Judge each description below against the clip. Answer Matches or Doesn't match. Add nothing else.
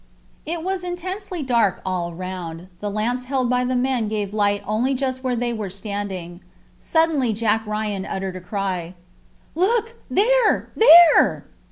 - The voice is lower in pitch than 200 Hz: Doesn't match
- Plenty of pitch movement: Matches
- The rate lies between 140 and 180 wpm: Matches